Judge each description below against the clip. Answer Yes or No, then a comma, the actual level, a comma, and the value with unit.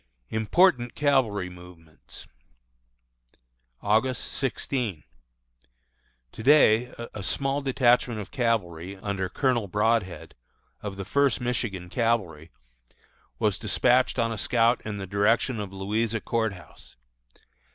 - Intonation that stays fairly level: No, average, 4.1 semitones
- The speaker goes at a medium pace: No, slow, 110 wpm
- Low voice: Yes, low, 110 Hz